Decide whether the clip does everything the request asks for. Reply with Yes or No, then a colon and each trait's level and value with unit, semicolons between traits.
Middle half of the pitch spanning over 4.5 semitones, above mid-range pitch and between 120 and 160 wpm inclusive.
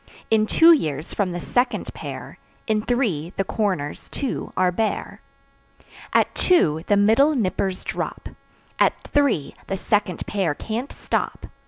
Yes: average, 5.1 semitones; high, 205 Hz; average, 140 wpm